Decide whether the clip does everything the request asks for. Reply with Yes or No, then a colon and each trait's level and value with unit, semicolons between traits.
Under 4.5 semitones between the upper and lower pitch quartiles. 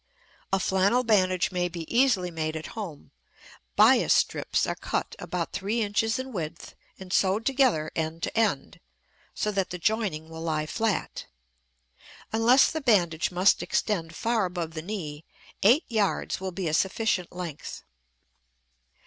No: average, 5.1 semitones